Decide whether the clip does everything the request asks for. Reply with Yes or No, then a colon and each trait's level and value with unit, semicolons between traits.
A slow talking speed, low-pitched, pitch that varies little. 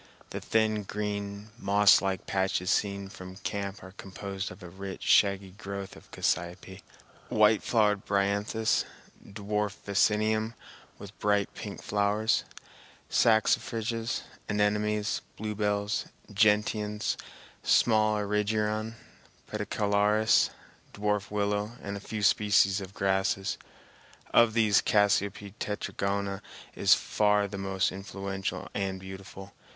Yes: slow, 105 wpm; low, 100 Hz; narrow, 1.3 semitones